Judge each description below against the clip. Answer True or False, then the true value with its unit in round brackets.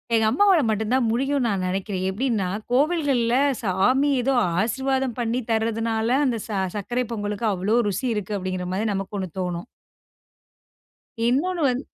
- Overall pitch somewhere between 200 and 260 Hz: True (230 Hz)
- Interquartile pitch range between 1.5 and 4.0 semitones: False (4.7 semitones)